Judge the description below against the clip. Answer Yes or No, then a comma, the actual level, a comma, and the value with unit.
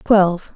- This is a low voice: No, high, 190 Hz